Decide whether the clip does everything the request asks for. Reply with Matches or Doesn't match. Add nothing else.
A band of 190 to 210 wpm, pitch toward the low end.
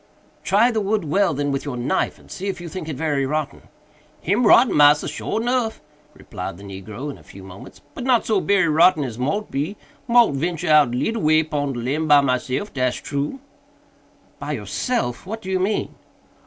Doesn't match